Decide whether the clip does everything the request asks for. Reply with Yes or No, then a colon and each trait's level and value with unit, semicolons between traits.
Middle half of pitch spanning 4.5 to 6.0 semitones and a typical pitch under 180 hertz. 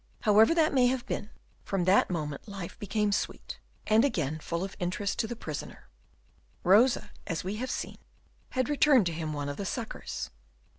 No: wide, 5.5 semitones; high, 205 Hz